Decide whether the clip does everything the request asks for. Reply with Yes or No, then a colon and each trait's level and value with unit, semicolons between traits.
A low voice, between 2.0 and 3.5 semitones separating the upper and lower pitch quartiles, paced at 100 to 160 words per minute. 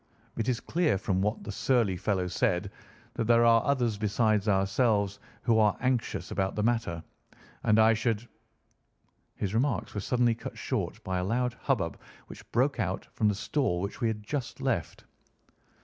No: low, 110 Hz; average, 3.2 semitones; average, 170 wpm